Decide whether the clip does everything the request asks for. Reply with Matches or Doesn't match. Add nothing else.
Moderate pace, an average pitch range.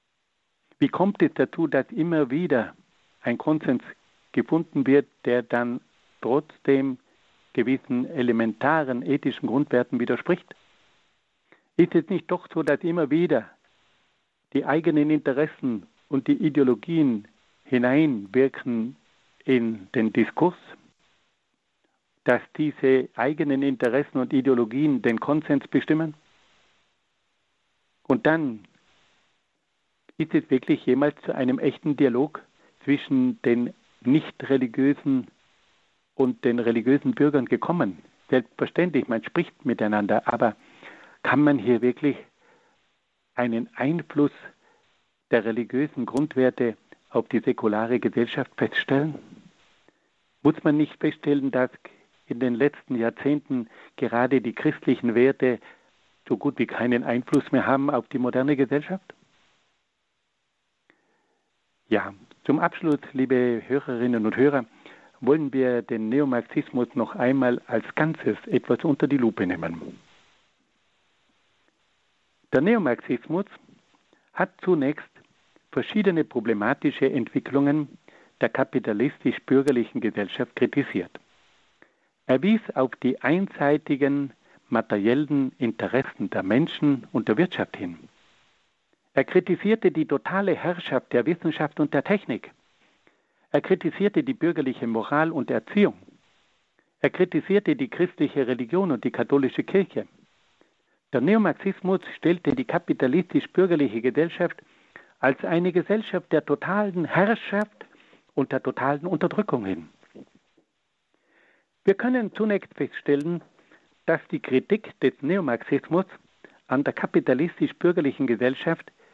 Doesn't match